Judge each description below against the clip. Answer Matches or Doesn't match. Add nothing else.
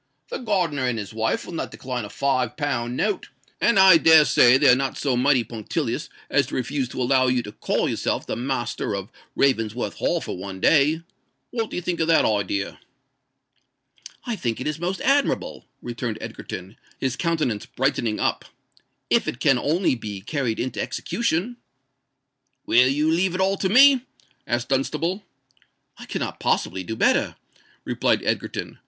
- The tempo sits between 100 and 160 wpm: Doesn't match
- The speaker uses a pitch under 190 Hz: Matches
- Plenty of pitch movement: Matches